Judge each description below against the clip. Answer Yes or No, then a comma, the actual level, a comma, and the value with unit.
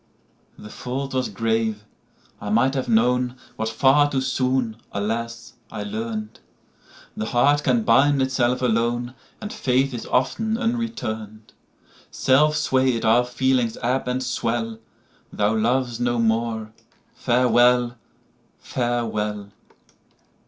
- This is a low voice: Yes, low, 120 Hz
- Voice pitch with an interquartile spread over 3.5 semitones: No, average, 2.7 semitones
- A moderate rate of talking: No, slow, 100 wpm